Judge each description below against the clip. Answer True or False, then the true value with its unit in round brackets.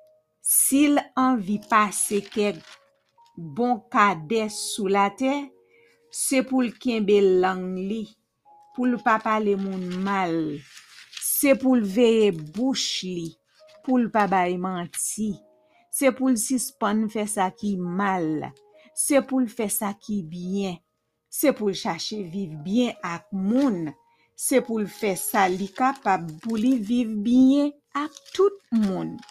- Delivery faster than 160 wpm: False (145 wpm)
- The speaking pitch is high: True (215 Hz)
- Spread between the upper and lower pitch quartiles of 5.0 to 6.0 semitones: True (5.3 semitones)